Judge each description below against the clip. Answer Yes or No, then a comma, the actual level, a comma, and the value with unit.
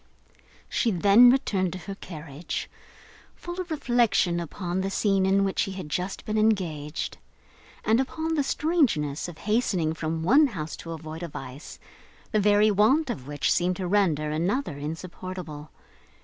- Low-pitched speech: No, medium, 185 Hz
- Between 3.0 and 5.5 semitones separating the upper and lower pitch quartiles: Yes, average, 5.2 semitones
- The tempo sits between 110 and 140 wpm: No, average, 155 wpm